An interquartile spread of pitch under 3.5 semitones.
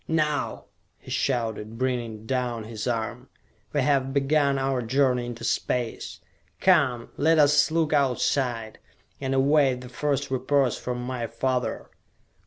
Yes: average, 2.8 semitones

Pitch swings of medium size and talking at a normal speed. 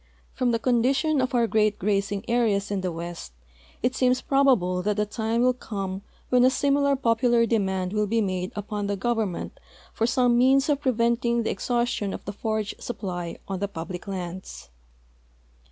Yes: average, 3.9 semitones; average, 175 wpm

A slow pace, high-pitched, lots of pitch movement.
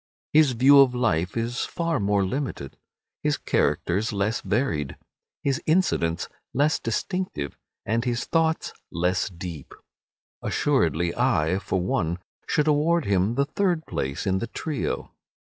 No: slow, 130 wpm; low, 115 Hz; wide, 8.1 semitones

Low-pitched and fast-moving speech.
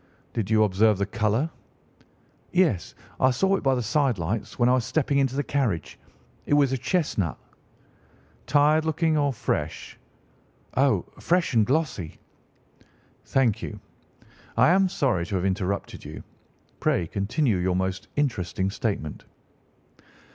No: low, 120 Hz; average, 140 wpm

